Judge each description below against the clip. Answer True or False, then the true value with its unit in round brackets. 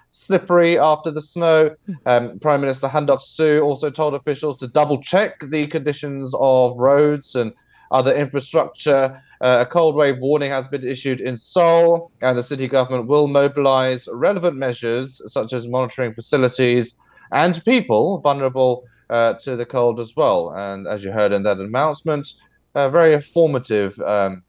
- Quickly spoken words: False (155 wpm)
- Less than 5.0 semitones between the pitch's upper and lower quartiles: True (3.4 semitones)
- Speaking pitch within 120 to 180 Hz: True (135 Hz)